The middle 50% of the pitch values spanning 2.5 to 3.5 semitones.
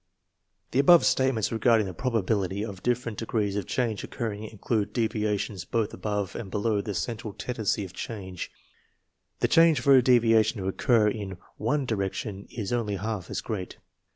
Yes: average, 2.8 semitones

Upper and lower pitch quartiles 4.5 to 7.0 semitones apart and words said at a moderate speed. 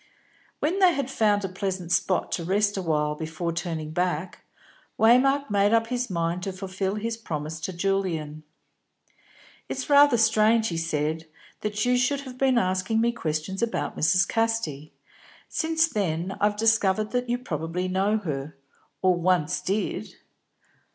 Yes: average, 5.3 semitones; average, 150 wpm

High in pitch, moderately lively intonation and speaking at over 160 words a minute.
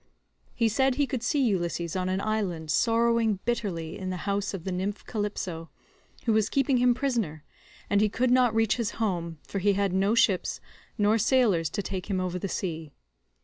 Yes: high, 205 Hz; average, 4.2 semitones; average, 190 wpm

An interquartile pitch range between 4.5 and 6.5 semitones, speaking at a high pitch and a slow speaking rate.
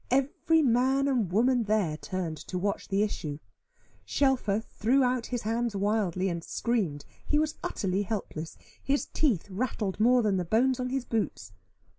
No: average, 4.8 semitones; high, 220 Hz; average, 160 wpm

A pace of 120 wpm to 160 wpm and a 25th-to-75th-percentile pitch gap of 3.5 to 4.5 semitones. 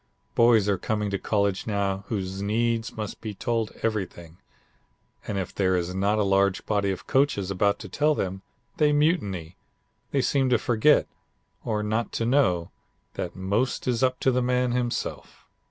No: average, 170 wpm; average, 3.8 semitones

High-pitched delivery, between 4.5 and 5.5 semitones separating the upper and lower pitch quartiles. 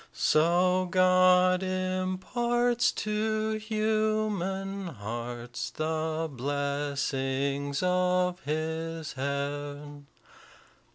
No: medium, 175 Hz; average, 4.8 semitones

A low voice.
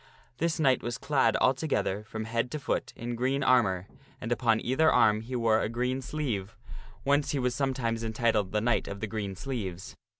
Yes: low, 120 Hz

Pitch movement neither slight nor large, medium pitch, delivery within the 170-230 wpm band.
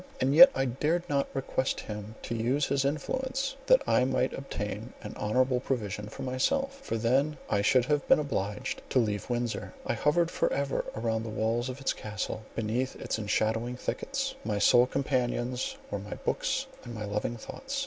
No: average, 4.0 semitones; low, 125 Hz; average, 180 wpm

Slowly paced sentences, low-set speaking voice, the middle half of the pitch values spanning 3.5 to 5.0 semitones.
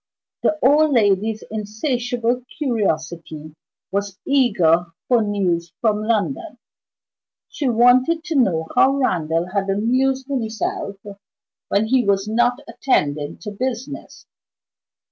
No: slow, 105 wpm; high, 220 Hz; average, 4.7 semitones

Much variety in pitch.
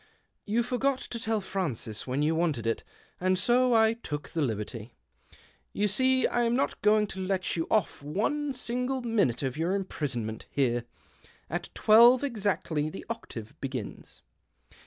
Yes: wide, 8.7 semitones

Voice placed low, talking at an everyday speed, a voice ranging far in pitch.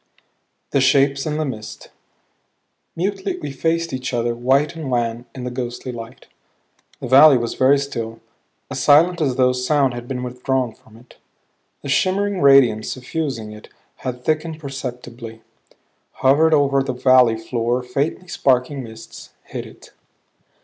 No: low, 130 Hz; average, 145 wpm; average, 2.9 semitones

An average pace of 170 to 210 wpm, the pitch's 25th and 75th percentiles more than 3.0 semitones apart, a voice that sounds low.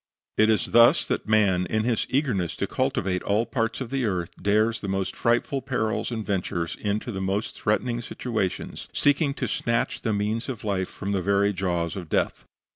Yes: average, 195 wpm; average, 3.4 semitones; low, 105 Hz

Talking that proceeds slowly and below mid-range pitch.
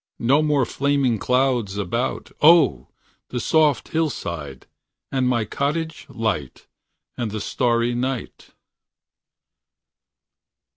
Yes: slow, 90 wpm; low, 125 Hz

